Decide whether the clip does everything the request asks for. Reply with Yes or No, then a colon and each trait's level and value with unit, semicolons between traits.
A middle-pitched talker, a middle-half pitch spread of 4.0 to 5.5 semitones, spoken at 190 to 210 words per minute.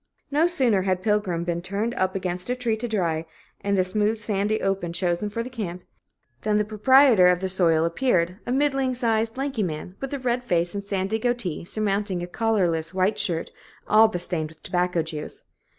No: high, 200 Hz; average, 4.3 semitones; average, 195 wpm